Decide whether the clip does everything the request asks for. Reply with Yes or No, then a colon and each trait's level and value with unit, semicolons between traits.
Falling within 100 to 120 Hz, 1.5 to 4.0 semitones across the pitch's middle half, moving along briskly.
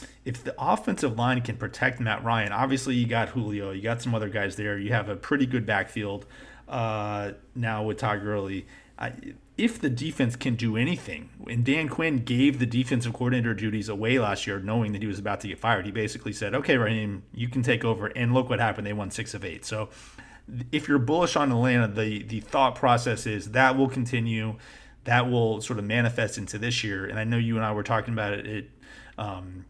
Yes: low, 115 Hz; average, 3.2 semitones; fast, 210 wpm